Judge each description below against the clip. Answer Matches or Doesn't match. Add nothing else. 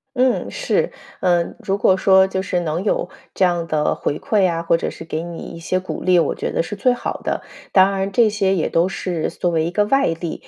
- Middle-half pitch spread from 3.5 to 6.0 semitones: Doesn't match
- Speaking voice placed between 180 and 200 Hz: Matches